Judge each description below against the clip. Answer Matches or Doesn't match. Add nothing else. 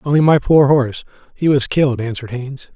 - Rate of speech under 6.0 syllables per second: Doesn't match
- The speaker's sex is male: Matches